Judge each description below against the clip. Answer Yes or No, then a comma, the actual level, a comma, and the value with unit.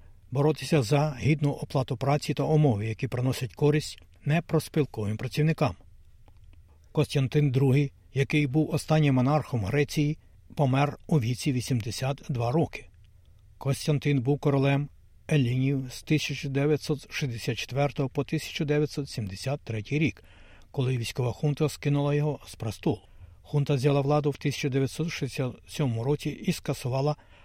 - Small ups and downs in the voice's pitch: No, average, 3.7 semitones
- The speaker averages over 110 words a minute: No, slow, 105 wpm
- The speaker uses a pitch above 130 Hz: Yes, medium, 140 Hz